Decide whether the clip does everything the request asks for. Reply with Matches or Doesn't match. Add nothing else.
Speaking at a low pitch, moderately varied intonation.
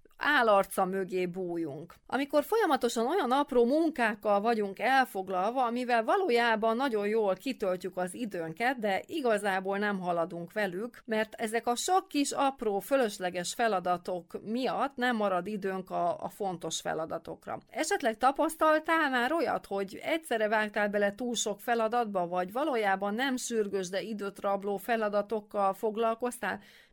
Doesn't match